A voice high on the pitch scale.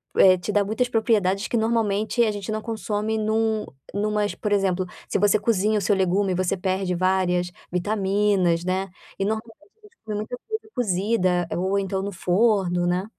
Yes: high, 200 Hz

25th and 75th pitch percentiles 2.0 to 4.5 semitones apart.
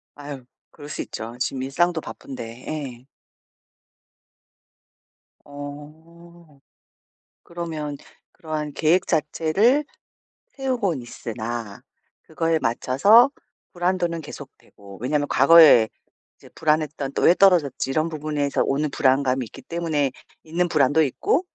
Yes: average, 3.8 semitones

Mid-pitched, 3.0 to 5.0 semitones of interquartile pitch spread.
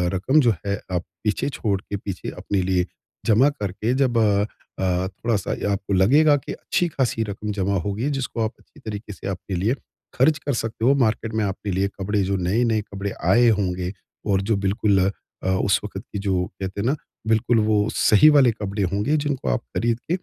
No: low, 105 Hz; average, 3.5 semitones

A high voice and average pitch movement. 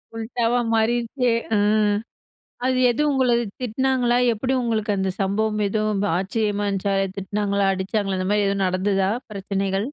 Yes: high, 210 Hz; average, 3.2 semitones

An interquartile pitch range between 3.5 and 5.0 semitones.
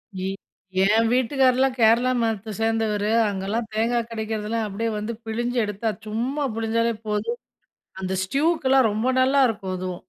No: average, 2.9 semitones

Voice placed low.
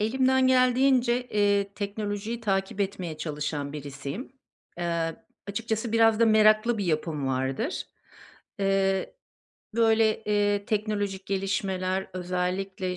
No: high, 200 Hz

